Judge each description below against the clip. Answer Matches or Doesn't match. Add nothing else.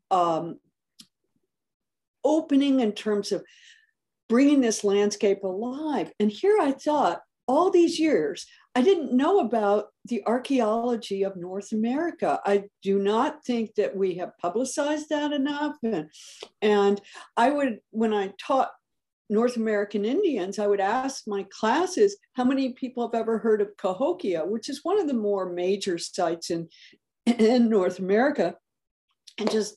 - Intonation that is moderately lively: Doesn't match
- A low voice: Doesn't match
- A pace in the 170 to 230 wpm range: Doesn't match